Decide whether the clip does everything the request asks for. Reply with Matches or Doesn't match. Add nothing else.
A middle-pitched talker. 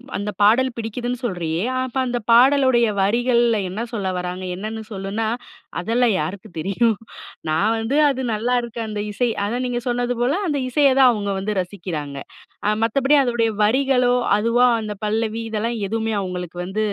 Doesn't match